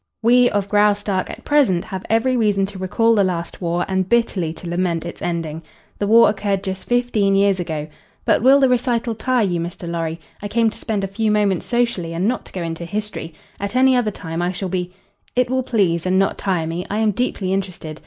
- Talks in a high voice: Yes, high, 195 Hz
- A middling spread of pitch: Yes, average, 4.4 semitones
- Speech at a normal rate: No, fast, 225 wpm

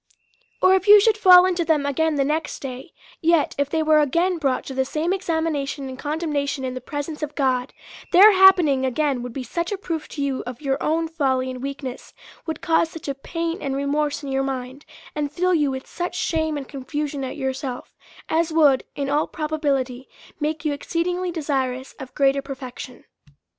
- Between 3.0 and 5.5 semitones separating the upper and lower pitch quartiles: Yes, average, 3.4 semitones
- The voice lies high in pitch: Yes, very high, 290 Hz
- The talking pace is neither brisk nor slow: Yes, average, 195 wpm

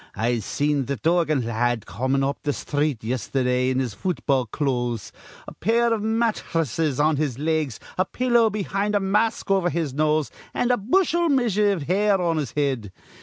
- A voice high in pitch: No, medium, 155 Hz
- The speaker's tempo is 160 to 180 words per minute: Yes, average, 175 wpm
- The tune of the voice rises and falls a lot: Yes, wide, 7.7 semitones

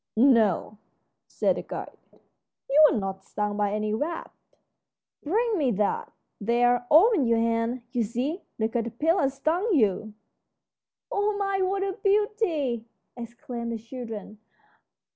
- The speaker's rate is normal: No, slow, 125 wpm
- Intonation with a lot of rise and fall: Yes, wide, 7.2 semitones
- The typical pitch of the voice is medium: No, high, 245 Hz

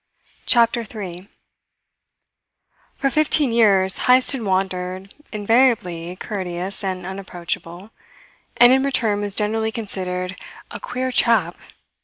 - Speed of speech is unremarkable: No, slow, 105 wpm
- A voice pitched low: No, high, 200 Hz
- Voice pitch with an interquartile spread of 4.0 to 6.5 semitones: Yes, average, 4.3 semitones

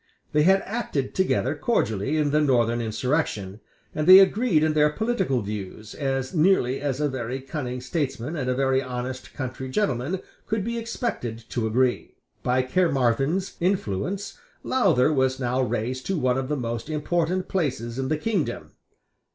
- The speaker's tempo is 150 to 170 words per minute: Yes, average, 160 wpm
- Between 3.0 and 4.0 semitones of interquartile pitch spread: No, wide, 5.4 semitones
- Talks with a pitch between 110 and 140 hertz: Yes, low, 135 Hz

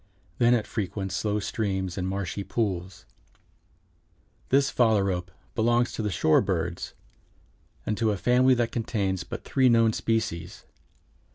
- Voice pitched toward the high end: No, low, 105 Hz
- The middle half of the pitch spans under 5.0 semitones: Yes, average, 3.7 semitones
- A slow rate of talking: Yes, slow, 130 wpm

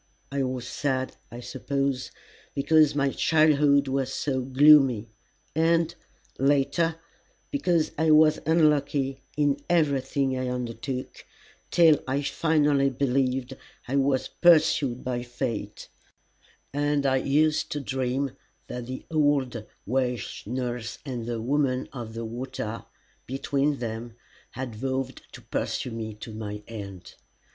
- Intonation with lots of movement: No, average, 2.9 semitones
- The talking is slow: Yes, slow, 120 wpm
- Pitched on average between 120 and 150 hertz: Yes, low, 135 Hz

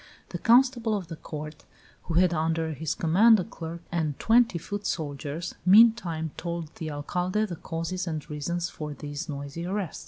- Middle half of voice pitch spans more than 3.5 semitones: No, average, 3.1 semitones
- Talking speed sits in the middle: Yes, average, 175 wpm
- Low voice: No, medium, 170 Hz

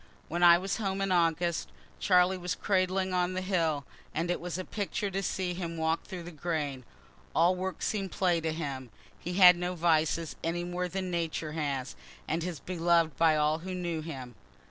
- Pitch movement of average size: No, narrow, 2.3 semitones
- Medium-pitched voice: Yes, medium, 175 Hz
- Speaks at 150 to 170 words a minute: No, average, 190 wpm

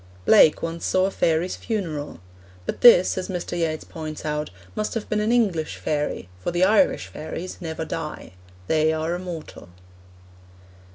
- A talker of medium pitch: Yes, medium, 165 Hz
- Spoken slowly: No, average, 155 wpm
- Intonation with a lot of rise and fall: No, average, 3.0 semitones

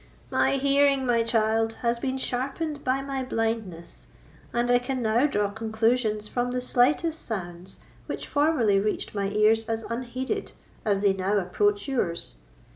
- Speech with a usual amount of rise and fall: Yes, average, 3.7 semitones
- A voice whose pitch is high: Yes, high, 230 Hz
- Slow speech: No, average, 150 wpm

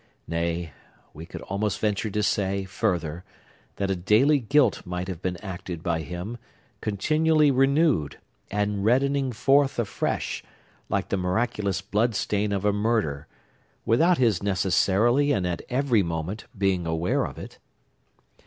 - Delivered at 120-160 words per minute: Yes, average, 140 wpm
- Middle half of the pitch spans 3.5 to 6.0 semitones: Yes, average, 5.0 semitones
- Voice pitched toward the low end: Yes, low, 100 Hz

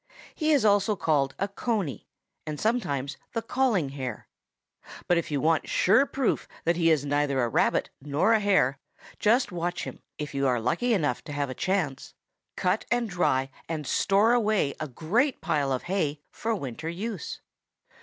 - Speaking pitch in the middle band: Yes, medium, 170 Hz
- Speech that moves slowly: No, average, 175 wpm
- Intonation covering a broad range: Yes, wide, 7.1 semitones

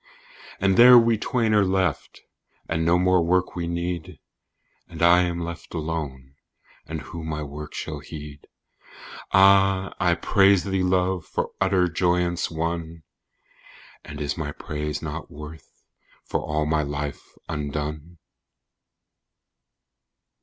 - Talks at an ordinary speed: No, slow, 125 wpm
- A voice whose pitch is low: Yes, very low, 85 Hz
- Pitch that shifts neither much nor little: Yes, average, 3.3 semitones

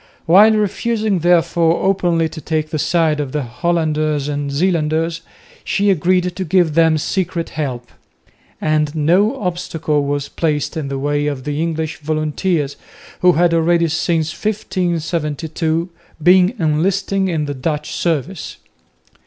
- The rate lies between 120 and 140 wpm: Yes, slow, 135 wpm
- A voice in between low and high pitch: Yes, medium, 160 Hz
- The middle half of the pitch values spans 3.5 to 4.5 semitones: No, average, 2.9 semitones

